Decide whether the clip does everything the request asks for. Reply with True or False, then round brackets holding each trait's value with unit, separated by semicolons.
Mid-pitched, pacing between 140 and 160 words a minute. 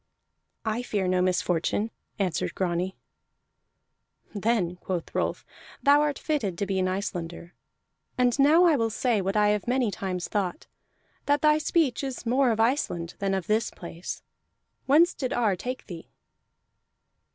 False (210 Hz; 150 wpm)